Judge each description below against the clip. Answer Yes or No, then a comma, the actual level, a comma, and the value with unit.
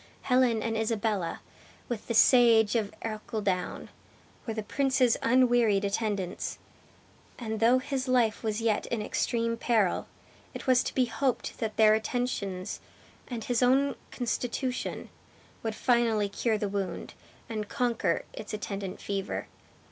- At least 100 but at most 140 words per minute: Yes, slow, 135 wpm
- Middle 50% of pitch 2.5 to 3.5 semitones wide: Yes, average, 2.8 semitones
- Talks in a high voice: Yes, high, 225 Hz